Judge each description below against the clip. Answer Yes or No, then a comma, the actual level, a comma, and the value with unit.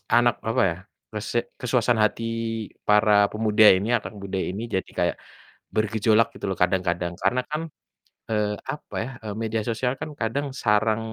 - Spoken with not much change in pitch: Yes, narrow, 2.2 semitones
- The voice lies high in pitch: No, low, 110 Hz